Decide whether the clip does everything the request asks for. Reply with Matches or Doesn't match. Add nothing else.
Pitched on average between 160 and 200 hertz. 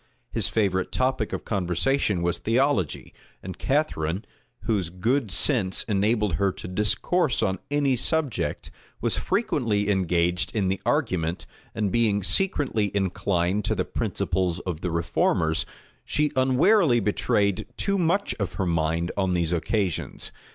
Doesn't match